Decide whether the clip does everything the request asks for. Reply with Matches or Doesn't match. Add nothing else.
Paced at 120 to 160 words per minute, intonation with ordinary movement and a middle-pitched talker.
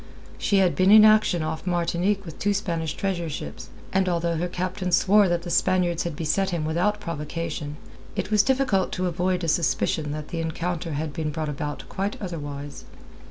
Doesn't match